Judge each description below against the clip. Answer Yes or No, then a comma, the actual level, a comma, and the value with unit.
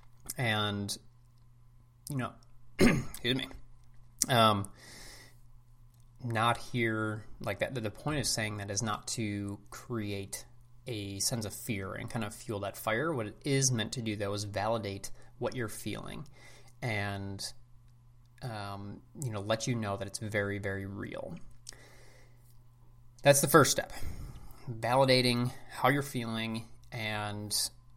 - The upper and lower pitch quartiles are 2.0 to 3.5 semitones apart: Yes, narrow, 2.4 semitones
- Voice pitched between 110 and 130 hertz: Yes, low, 120 Hz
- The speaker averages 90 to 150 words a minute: Yes, slow, 135 wpm